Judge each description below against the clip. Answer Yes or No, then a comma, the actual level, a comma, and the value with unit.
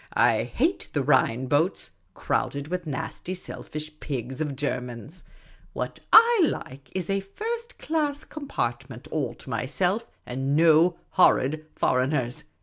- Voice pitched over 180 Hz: No, medium, 155 Hz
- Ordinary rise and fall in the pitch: No, wide, 6.4 semitones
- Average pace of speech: No, slow, 125 wpm